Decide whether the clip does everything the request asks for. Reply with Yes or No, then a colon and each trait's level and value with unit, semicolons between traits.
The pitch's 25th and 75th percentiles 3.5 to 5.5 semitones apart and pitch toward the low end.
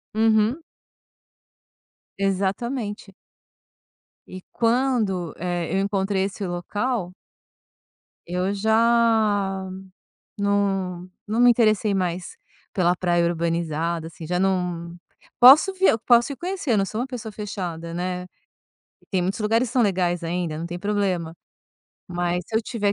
No: average, 3.9 semitones; high, 195 Hz